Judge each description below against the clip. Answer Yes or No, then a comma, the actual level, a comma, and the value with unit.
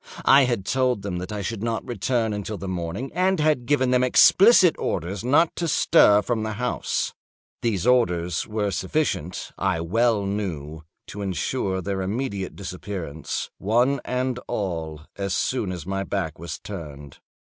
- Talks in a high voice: No, low, 100 Hz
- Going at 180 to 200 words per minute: No, average, 155 wpm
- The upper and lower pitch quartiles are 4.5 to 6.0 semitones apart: Yes, wide, 5.4 semitones